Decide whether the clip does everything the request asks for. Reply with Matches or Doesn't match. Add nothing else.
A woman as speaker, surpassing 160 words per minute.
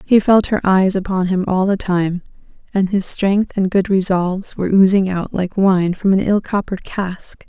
Matches